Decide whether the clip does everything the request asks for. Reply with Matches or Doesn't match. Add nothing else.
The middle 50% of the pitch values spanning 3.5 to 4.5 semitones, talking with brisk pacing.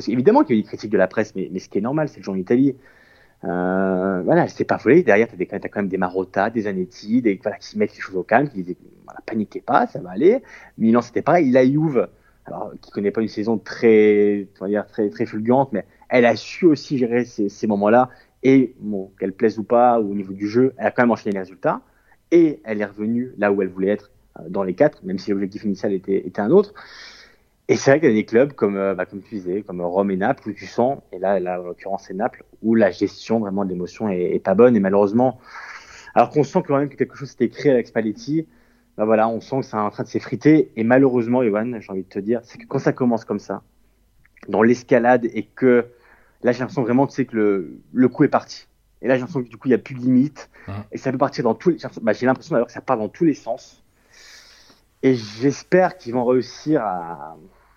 Matches